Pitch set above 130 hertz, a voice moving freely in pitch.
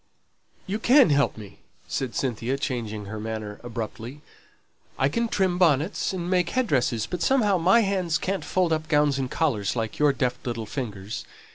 Yes: medium, 140 Hz; wide, 7.9 semitones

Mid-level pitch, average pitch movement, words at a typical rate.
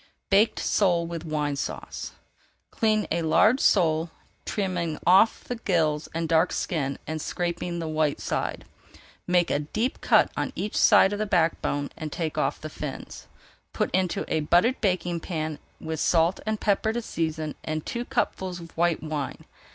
Yes: medium, 170 Hz; average, 3.5 semitones; average, 165 wpm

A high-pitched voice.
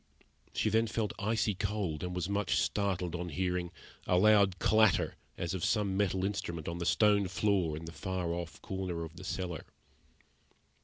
No: very low, 95 Hz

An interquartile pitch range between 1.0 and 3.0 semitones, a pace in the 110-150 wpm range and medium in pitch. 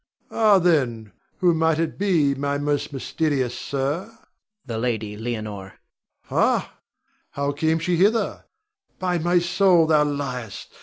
No: wide, 5.6 semitones; average, 145 wpm; medium, 145 Hz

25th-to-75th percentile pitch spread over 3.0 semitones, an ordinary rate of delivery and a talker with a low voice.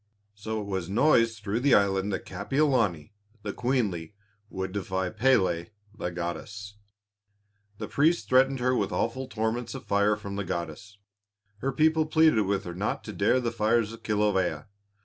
Yes: average, 4.3 semitones; average, 160 wpm; low, 105 Hz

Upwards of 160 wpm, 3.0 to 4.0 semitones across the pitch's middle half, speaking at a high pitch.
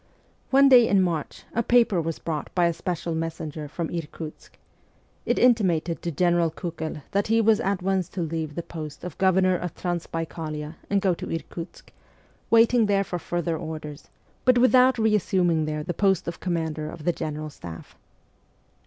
No: average, 170 wpm; average, 3.5 semitones; medium, 170 Hz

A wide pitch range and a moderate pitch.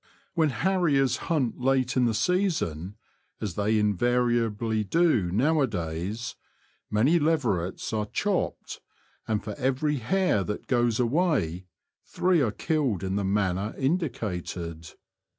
No: wide, 6.7 semitones; low, 120 Hz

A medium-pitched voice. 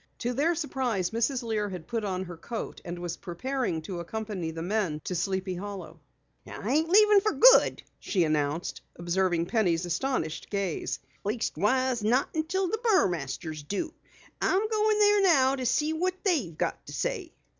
No: high, 215 Hz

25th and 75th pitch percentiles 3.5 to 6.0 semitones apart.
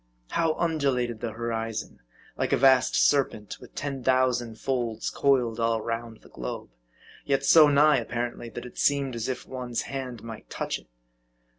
No: average, 2.9 semitones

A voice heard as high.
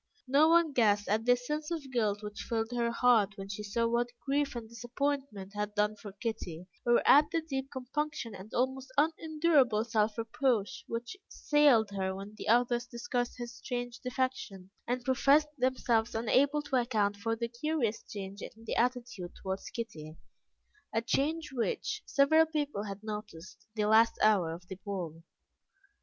Yes: high, 235 Hz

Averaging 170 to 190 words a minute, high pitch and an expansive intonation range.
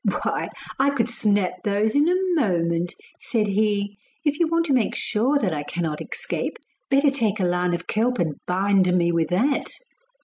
Yes: average, 180 wpm; high, 205 Hz; wide, 6.7 semitones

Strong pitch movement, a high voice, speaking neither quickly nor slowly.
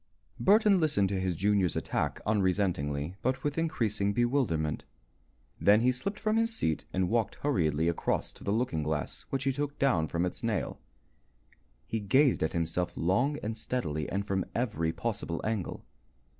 No: wide, 7.2 semitones; low, 105 Hz; average, 160 wpm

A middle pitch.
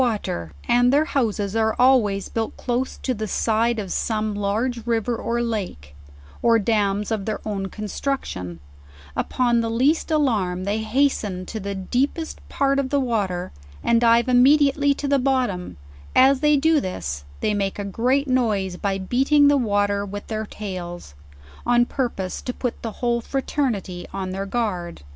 No: high, 225 Hz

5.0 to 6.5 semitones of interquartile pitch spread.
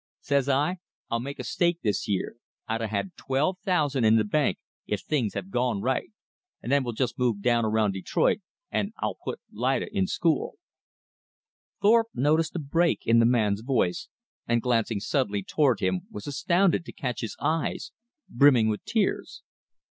Yes: average, 5.3 semitones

